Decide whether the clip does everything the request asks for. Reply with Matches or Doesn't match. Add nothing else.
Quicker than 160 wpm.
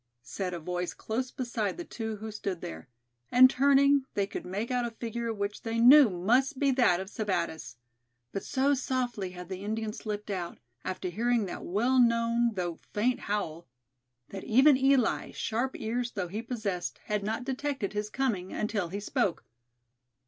Matches